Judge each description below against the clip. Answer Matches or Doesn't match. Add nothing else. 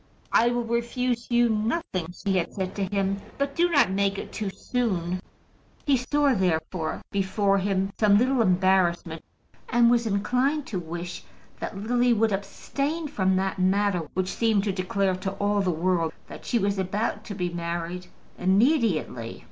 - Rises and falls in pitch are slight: Doesn't match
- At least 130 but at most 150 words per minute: Doesn't match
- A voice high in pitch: Matches